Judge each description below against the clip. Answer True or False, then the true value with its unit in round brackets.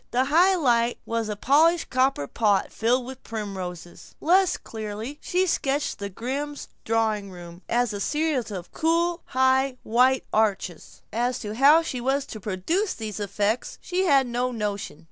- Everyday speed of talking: True (160 wpm)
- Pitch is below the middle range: False (245 Hz)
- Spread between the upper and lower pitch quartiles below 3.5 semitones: False (5.2 semitones)